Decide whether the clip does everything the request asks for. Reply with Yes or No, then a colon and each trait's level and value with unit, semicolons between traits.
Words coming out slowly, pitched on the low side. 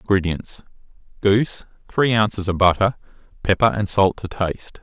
Yes: slow, 125 wpm; low, 100 Hz